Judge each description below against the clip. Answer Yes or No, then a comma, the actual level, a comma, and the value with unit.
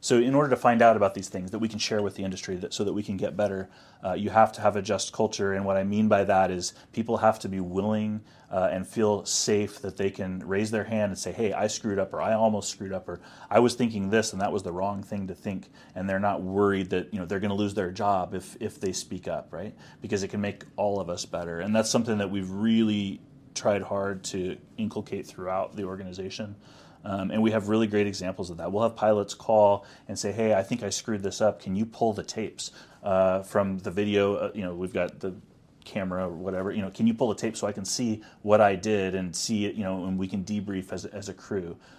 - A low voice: Yes, low, 100 Hz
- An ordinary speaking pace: No, fast, 265 wpm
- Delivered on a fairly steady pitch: Yes, narrow, 2.2 semitones